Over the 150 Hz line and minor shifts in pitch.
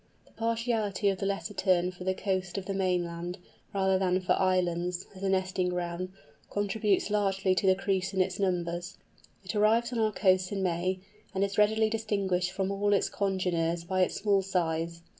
Yes: high, 190 Hz; narrow, 1.9 semitones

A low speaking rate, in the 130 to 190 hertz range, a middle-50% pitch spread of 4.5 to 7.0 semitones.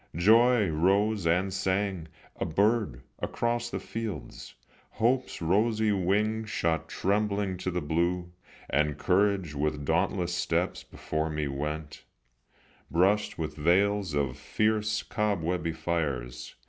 No: slow, 115 wpm; very low, 90 Hz; average, 5.0 semitones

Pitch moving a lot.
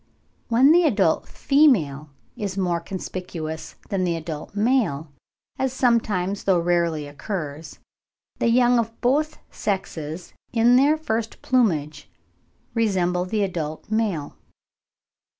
Yes: wide, 6.1 semitones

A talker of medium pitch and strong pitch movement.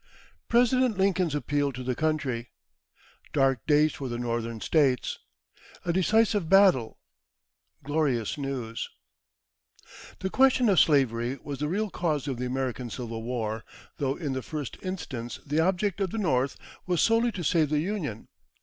Yes: medium, 145 Hz; wide, 6.7 semitones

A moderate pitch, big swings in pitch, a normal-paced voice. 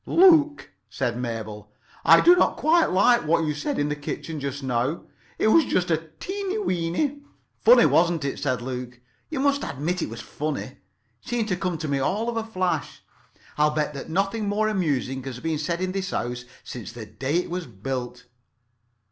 Yes: medium, 160 Hz; wide, 8.1 semitones; average, 190 wpm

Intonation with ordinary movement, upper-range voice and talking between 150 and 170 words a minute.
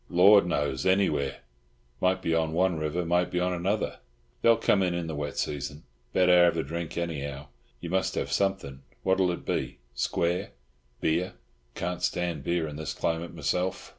No: average, 3.0 semitones; very low, 85 Hz; average, 165 wpm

